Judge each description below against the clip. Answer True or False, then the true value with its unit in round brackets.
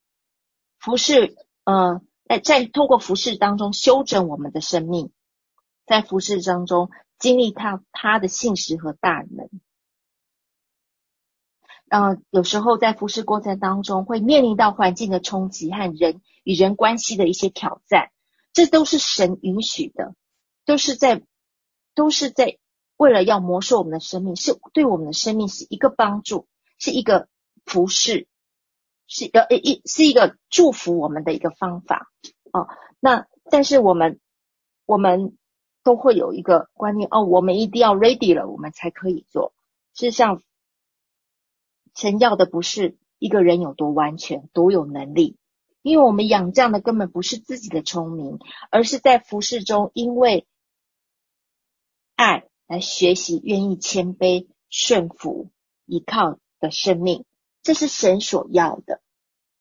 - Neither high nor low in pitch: False (200 Hz)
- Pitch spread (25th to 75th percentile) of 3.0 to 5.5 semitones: True (5.2 semitones)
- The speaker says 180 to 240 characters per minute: True (220 characters per minute)